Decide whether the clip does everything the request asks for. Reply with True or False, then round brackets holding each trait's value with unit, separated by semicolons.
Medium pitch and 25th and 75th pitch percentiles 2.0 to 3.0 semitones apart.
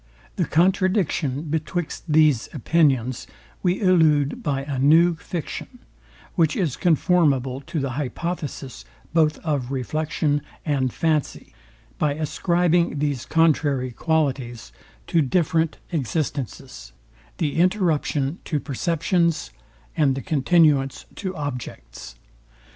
False (150 Hz; 3.6 semitones)